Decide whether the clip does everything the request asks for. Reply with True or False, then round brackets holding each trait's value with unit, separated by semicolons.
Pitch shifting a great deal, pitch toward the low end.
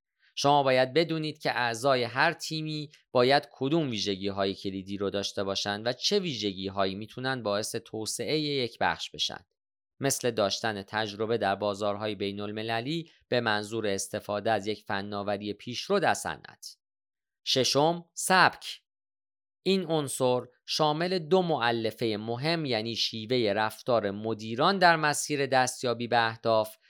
True (5.9 semitones; 120 Hz)